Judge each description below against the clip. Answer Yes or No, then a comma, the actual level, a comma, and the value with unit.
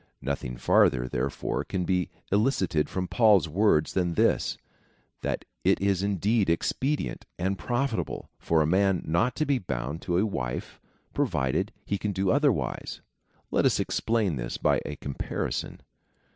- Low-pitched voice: Yes, very low, 95 Hz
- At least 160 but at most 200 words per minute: No, average, 150 wpm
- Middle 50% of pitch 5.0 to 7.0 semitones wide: Yes, wide, 5.6 semitones